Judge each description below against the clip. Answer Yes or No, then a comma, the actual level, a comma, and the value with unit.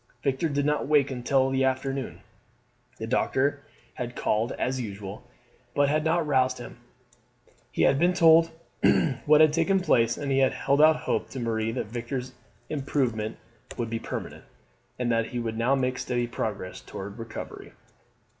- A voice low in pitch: Yes, low, 130 Hz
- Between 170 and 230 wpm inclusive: No, average, 160 wpm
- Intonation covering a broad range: No, average, 3.7 semitones